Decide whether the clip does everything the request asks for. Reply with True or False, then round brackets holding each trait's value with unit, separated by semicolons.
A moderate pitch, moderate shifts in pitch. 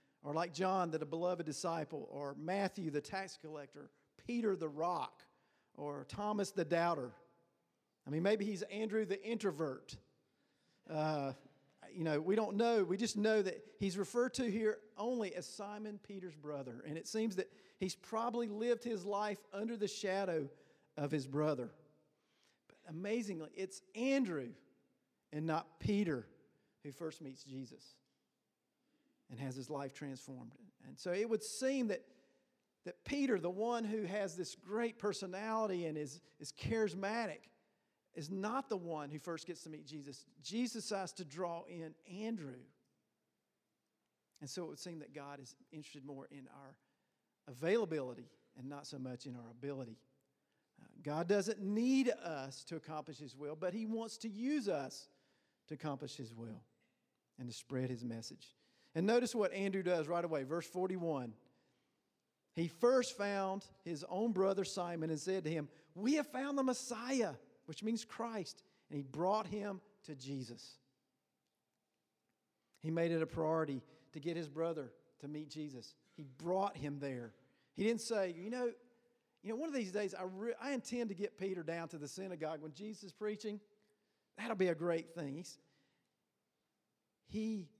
False (175 Hz; 6.0 semitones)